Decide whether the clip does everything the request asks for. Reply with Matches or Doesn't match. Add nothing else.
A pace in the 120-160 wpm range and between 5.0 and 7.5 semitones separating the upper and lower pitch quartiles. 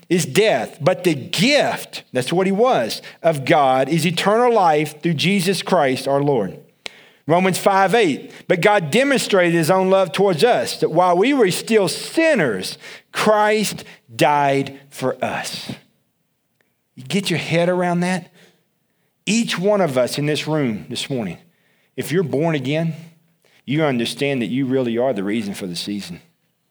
Matches